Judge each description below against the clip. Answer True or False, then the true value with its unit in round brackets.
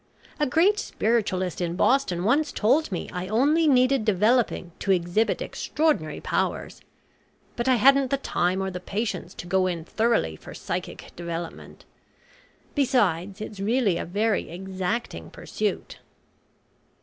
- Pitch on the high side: True (210 Hz)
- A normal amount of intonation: False (6.1 semitones)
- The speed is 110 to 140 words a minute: True (135 wpm)